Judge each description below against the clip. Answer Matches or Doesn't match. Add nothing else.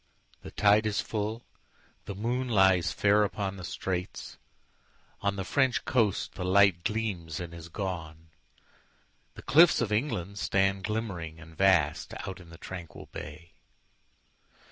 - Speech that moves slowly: Matches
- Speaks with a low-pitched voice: Matches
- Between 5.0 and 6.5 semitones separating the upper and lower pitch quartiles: Doesn't match